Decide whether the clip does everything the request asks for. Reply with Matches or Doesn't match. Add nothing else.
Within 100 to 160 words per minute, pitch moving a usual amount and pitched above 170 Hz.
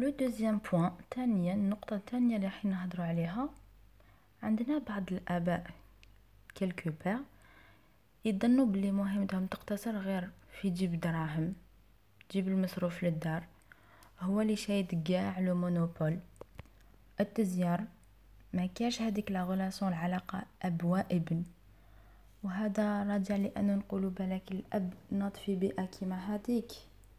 Matches